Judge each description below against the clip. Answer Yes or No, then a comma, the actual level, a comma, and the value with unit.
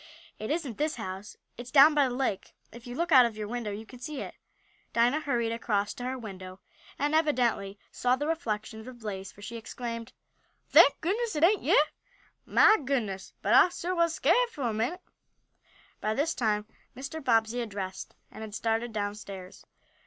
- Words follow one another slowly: No, average, 190 wpm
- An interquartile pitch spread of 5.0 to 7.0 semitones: Yes, wide, 5.4 semitones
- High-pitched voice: Yes, high, 235 Hz